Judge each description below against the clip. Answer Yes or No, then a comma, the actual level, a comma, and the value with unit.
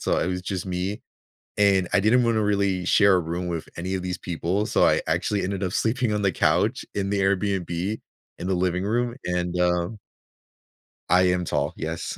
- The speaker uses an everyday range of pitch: No, narrow, 2.3 semitones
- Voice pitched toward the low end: Yes, very low, 95 Hz